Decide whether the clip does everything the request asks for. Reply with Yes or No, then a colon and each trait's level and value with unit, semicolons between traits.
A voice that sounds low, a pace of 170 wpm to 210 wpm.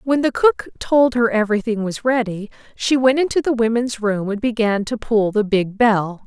No: high, 230 Hz; average, 200 wpm